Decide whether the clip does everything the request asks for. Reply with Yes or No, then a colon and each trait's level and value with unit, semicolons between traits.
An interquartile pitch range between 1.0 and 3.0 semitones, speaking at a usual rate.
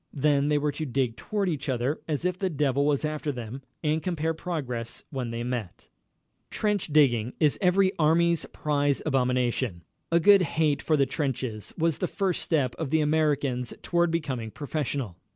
No: average, 4.2 semitones; average, 170 wpm